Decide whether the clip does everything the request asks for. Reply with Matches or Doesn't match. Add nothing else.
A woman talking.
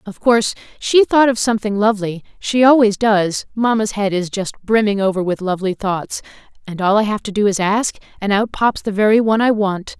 Matches